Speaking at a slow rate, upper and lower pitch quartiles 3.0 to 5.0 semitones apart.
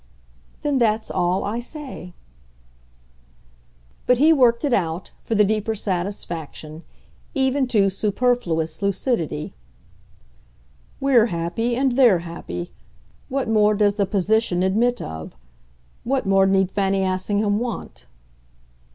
Yes: slow, 115 wpm; average, 4.7 semitones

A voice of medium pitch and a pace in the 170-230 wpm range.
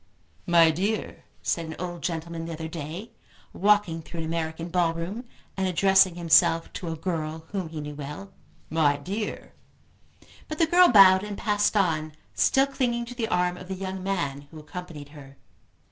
Yes: medium, 175 Hz; average, 175 wpm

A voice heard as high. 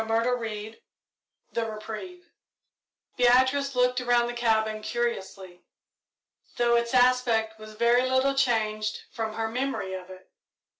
Yes: high, 235 Hz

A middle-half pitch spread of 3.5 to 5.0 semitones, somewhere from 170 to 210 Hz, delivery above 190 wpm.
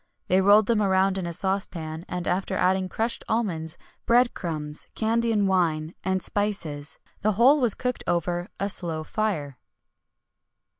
No: average, 4.1 semitones; high, 190 Hz; average, 145 wpm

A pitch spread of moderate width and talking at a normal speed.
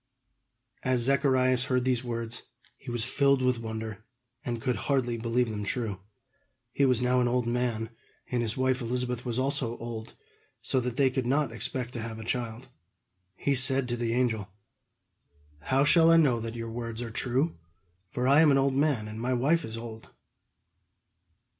No: narrow, 2.3 semitones; average, 180 wpm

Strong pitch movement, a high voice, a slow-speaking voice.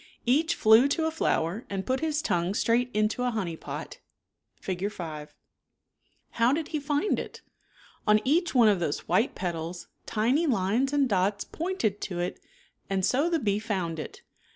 No: wide, 6.8 semitones; high, 220 Hz; average, 170 wpm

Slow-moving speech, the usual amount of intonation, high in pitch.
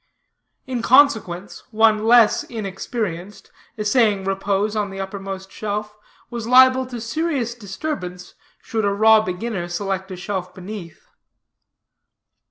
Yes: slow, 115 wpm; average, 3.2 semitones; high, 210 Hz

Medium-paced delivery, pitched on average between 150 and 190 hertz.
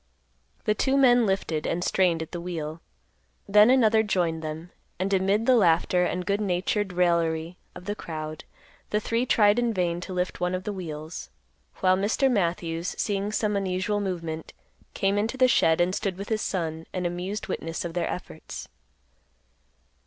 Yes: average, 170 wpm; medium, 185 Hz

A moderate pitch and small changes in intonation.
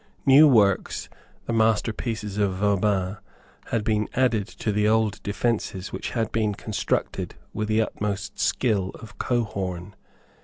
No: low, 105 Hz; narrow, 2.0 semitones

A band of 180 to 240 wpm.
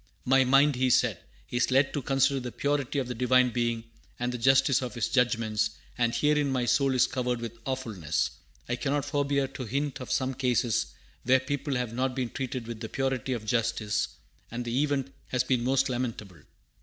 Yes: average, 195 wpm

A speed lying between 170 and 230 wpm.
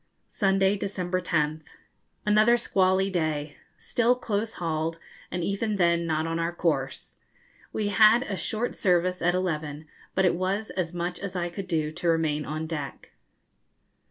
No: average, 155 wpm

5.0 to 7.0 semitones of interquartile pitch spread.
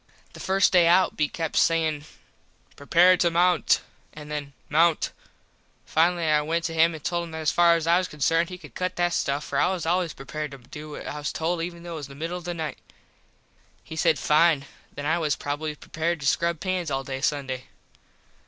No: narrow, 2.4 semitones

